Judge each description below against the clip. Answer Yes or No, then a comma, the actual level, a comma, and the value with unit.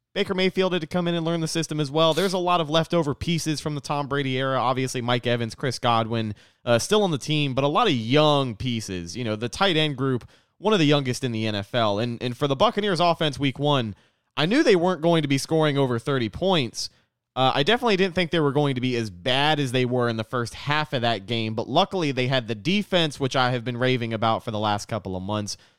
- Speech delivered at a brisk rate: Yes, fast, 260 wpm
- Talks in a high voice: No, low, 135 Hz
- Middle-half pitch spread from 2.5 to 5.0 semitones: No, wide, 5.4 semitones